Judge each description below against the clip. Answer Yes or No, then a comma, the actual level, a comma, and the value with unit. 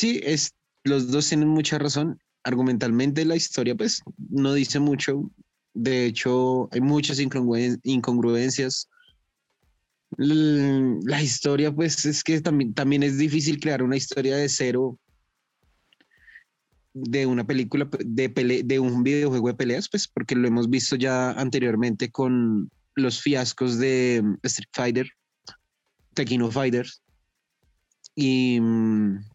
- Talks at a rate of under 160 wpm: Yes, slow, 125 wpm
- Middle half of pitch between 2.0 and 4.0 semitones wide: Yes, narrow, 2.6 semitones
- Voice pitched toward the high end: No, low, 130 Hz